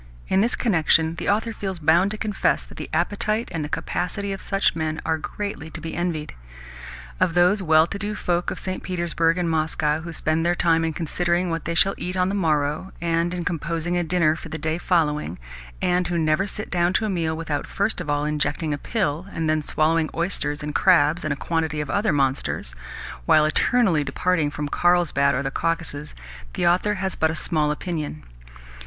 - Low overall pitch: No, medium, 165 Hz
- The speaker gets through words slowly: No, fast, 205 wpm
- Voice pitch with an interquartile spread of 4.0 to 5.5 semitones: No, average, 2.9 semitones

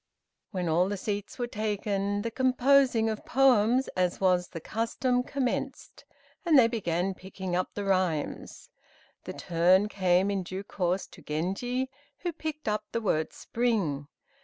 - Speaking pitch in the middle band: No, high, 205 Hz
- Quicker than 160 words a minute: No, average, 150 wpm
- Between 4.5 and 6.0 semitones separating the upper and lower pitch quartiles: Yes, average, 4.9 semitones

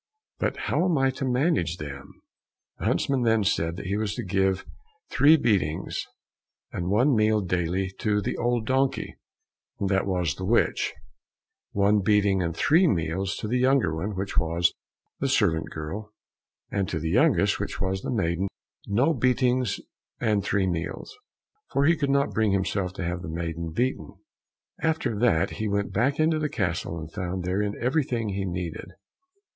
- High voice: No, low, 100 Hz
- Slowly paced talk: No, average, 170 wpm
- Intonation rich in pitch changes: Yes, wide, 5.7 semitones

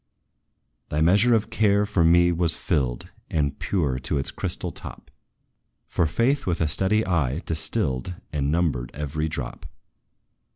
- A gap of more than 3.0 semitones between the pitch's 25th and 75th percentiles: Yes, average, 5.0 semitones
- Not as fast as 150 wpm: Yes, average, 140 wpm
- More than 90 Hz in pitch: No, very low, 80 Hz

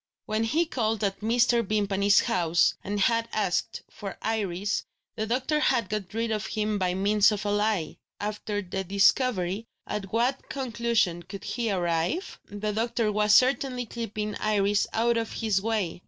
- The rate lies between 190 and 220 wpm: No, average, 165 wpm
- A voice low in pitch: No, high, 215 Hz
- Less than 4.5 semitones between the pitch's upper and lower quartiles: Yes, average, 2.7 semitones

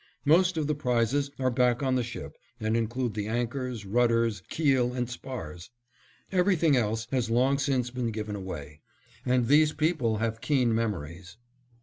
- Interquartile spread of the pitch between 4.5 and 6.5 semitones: No, average, 3.4 semitones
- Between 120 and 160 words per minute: Yes, average, 155 wpm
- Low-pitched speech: Yes, low, 120 Hz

